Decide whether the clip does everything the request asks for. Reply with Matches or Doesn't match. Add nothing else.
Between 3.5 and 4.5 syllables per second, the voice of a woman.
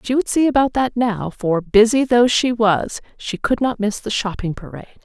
Doesn't match